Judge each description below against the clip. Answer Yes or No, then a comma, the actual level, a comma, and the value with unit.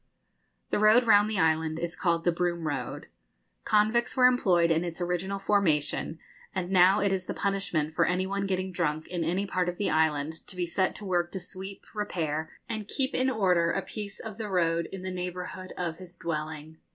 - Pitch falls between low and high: Yes, medium, 180 Hz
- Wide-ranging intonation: No, average, 3.1 semitones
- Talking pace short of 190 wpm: No, average, 200 wpm